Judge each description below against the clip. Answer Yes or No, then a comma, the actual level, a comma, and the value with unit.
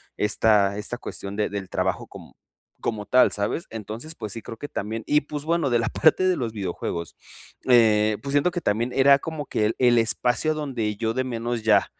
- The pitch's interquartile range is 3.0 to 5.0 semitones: Yes, average, 4.7 semitones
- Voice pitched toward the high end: No, low, 115 Hz